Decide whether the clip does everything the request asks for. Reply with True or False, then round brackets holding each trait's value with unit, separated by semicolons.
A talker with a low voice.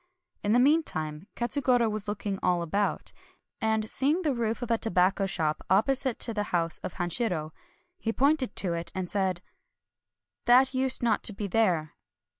False (215 Hz)